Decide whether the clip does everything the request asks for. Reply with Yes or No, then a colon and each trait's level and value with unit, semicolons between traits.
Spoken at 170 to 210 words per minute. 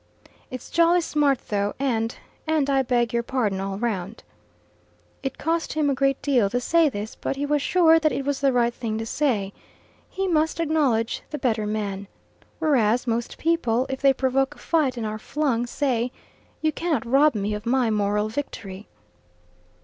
Yes: average, 180 wpm